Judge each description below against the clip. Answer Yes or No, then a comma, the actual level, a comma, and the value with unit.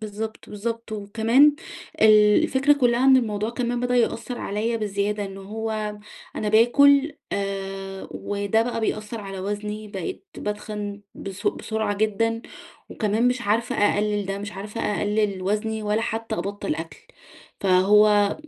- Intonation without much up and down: Yes, narrow, 2.0 semitones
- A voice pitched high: Yes, high, 210 Hz